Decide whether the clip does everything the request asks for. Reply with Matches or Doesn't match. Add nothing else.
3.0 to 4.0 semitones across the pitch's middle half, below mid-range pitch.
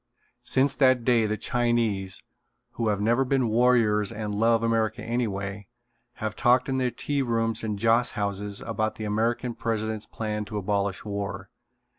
Doesn't match